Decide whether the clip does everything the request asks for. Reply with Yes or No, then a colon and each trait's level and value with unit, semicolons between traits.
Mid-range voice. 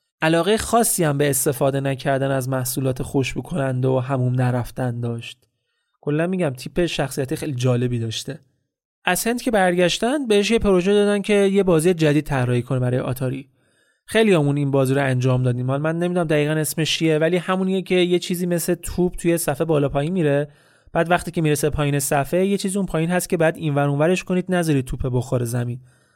Yes: medium, 150 Hz